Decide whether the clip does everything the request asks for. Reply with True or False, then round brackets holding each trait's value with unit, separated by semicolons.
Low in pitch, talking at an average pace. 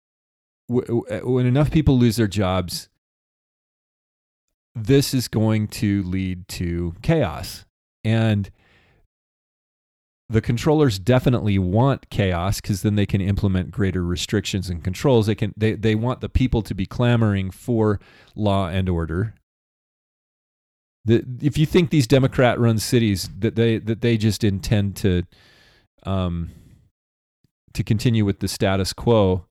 False (105 Hz; 130 wpm)